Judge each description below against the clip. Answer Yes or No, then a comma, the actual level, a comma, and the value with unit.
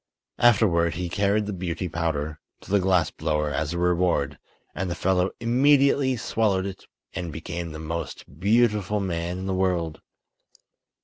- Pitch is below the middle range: Yes, very low, 90 Hz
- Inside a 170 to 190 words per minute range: No, average, 150 wpm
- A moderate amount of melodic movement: Yes, average, 3.5 semitones